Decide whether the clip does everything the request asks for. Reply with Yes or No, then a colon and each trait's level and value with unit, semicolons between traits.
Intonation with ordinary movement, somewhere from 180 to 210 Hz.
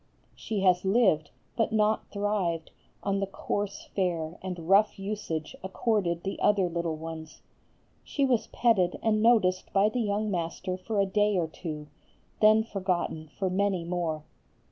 Yes: average, 3.6 semitones; high, 190 Hz